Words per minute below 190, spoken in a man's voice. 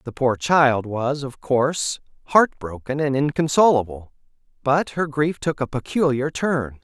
Yes: average, 140 wpm; male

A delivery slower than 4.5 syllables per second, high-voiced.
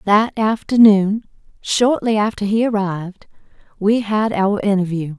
Yes: 4.3 syllables/s; high, 205 Hz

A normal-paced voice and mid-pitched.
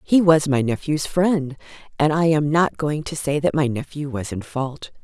No: fast, 215 wpm; medium, 145 Hz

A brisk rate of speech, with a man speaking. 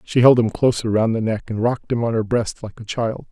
Yes: fast, 290 wpm; male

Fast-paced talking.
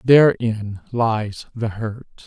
No: slow, 105 wpm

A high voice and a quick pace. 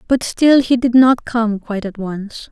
Yes: high, 230 Hz; fast, 215 wpm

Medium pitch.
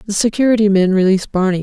No: high, 200 Hz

